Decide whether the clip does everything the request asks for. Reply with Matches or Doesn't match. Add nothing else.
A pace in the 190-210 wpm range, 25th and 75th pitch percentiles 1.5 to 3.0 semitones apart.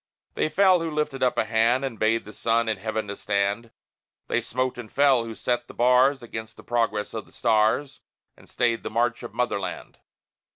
Matches